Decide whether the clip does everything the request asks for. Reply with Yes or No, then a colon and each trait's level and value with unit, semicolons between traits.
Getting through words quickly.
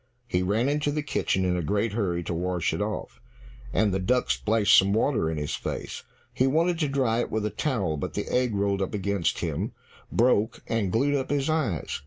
Yes: fast, 215 wpm